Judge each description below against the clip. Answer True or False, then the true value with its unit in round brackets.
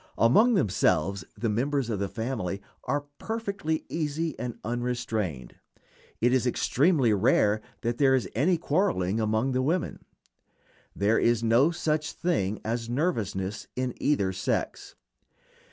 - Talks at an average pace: False (130 wpm)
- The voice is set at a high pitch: False (120 Hz)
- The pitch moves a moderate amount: False (5.8 semitones)